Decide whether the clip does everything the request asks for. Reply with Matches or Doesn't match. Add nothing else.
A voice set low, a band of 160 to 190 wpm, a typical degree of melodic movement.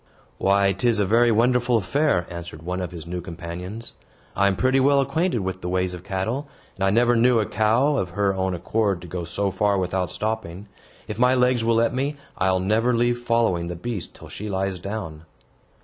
Doesn't match